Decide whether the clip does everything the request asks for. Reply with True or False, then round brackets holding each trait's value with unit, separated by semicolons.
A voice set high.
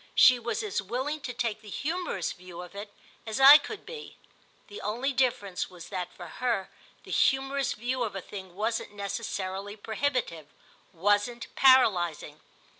True (220 Hz)